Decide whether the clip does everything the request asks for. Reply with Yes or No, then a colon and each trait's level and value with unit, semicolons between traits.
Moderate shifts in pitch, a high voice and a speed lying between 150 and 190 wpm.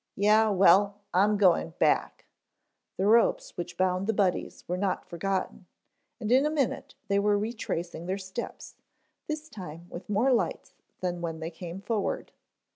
Yes: average, 3.2 semitones; high, 195 Hz; average, 155 wpm